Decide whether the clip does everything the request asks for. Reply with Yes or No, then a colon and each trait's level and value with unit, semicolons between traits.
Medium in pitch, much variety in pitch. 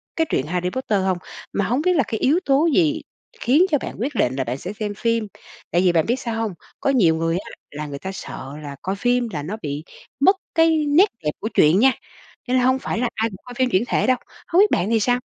No: high, 225 Hz; wide, 6.8 semitones